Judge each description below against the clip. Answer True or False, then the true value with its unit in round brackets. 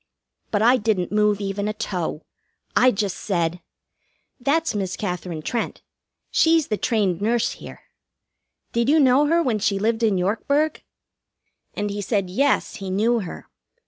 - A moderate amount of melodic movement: True (3.8 semitones)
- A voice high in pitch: True (210 Hz)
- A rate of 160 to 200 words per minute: False (150 wpm)